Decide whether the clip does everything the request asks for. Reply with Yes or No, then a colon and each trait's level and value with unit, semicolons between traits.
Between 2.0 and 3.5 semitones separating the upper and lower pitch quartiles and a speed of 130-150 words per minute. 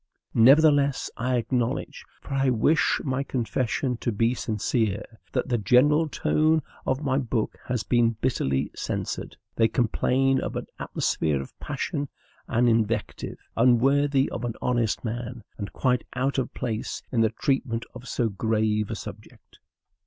Yes: average, 2.9 semitones; average, 145 wpm